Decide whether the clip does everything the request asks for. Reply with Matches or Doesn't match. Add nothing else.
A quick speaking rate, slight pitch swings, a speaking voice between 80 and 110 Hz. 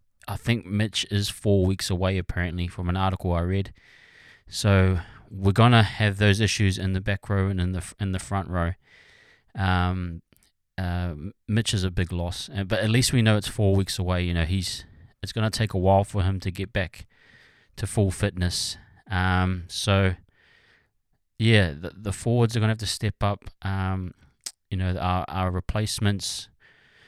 Doesn't match